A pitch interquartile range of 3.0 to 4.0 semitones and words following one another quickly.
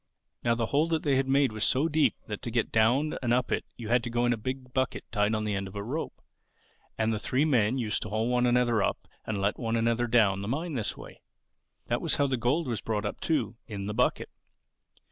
Yes: average, 3.3 semitones; fast, 250 wpm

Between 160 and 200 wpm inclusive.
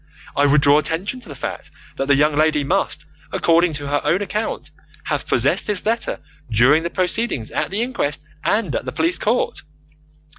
Yes: average, 185 wpm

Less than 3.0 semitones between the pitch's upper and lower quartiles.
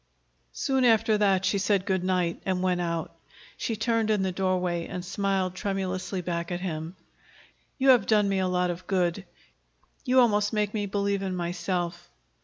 Yes: narrow, 2.4 semitones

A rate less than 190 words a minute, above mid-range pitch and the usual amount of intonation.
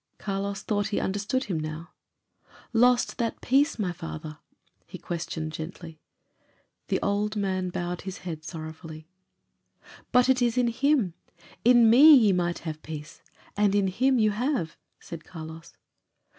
No: average, 140 wpm; high, 195 Hz; wide, 6.2 semitones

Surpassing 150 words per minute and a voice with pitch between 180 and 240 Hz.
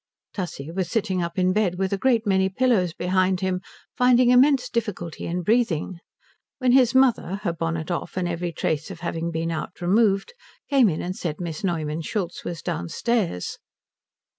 Yes: average, 170 wpm; medium, 185 Hz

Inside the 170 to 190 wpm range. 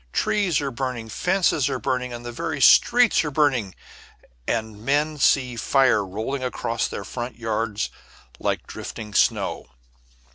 No: slow, 135 wpm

